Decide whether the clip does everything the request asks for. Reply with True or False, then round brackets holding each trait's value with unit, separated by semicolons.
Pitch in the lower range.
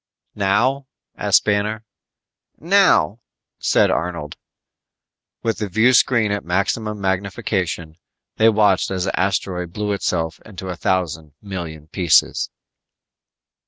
True (95 Hz)